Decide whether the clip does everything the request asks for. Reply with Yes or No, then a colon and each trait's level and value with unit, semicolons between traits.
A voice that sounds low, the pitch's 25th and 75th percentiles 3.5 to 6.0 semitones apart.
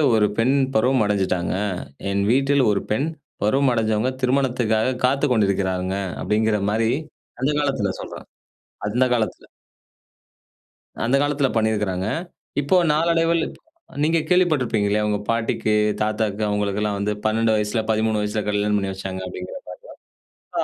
Yes: low, 110 Hz; average, 3.9 semitones